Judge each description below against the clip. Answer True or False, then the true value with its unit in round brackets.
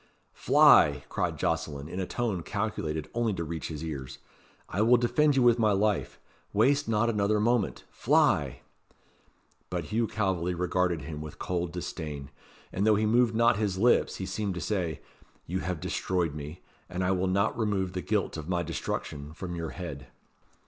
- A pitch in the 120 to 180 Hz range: False (95 Hz)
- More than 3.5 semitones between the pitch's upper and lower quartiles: True (4.6 semitones)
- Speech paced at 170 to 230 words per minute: True (175 wpm)